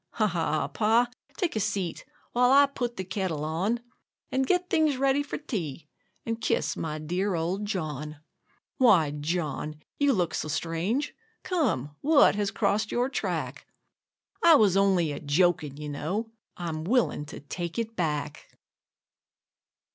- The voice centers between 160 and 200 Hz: Yes, high, 190 Hz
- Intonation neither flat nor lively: No, wide, 7.3 semitones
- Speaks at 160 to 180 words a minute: No, average, 145 wpm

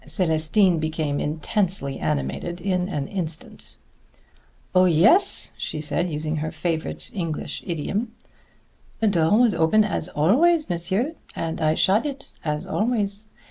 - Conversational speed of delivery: No, slow, 130 wpm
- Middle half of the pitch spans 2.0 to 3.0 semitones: No, average, 4.6 semitones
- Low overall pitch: No, medium, 175 Hz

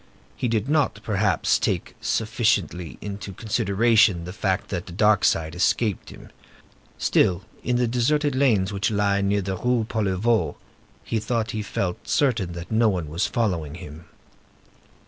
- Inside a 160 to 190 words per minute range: No, average, 150 wpm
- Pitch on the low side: Yes, low, 105 Hz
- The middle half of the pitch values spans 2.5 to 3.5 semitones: No, average, 3.9 semitones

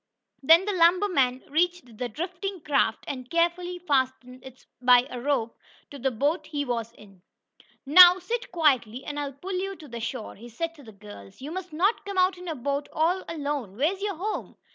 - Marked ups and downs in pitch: Yes, wide, 6.0 semitones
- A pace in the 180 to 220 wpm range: Yes, average, 200 wpm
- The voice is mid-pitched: No, very high, 290 Hz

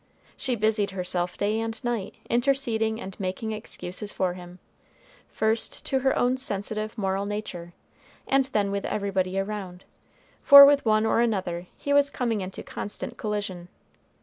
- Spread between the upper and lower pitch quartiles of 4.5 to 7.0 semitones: No, average, 3.5 semitones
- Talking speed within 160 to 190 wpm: No, average, 150 wpm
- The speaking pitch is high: Yes, high, 210 Hz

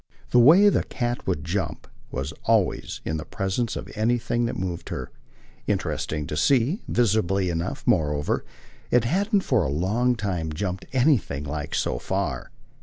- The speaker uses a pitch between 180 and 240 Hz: No, low, 100 Hz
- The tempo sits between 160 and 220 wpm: No, average, 150 wpm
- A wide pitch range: Yes, wide, 7.1 semitones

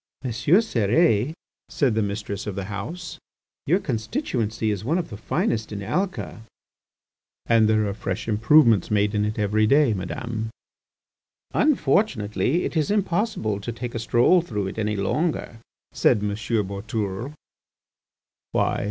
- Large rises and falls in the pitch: Yes, wide, 5.9 semitones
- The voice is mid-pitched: No, low, 110 Hz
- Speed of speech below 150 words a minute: Yes, average, 140 wpm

